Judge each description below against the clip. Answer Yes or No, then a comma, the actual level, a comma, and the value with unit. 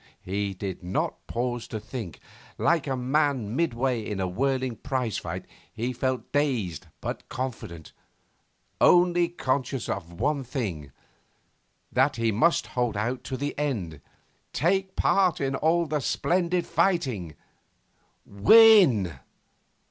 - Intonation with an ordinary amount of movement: No, wide, 6.3 semitones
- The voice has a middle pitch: No, low, 130 Hz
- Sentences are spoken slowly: Yes, slow, 125 wpm